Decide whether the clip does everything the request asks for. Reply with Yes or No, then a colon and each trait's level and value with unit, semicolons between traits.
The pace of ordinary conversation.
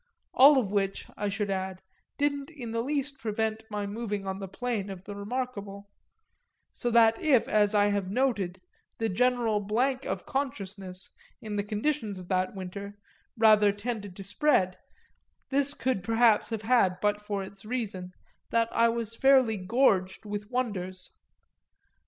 Yes: average, 160 wpm